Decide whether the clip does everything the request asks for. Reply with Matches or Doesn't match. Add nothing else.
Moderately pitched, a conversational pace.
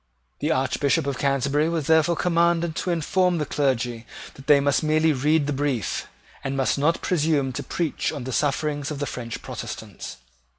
Matches